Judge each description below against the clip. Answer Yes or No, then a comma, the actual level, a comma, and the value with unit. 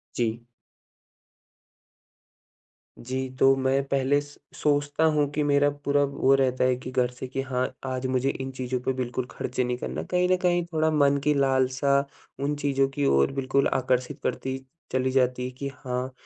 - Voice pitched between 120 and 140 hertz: Yes, low, 135 Hz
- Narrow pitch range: Yes, narrow, 1.8 semitones